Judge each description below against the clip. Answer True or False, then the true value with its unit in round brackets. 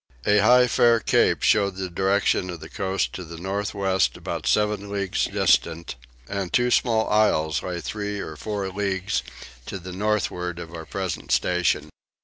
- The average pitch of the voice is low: True (95 Hz)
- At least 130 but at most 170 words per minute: True (165 wpm)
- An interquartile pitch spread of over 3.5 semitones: False (2.5 semitones)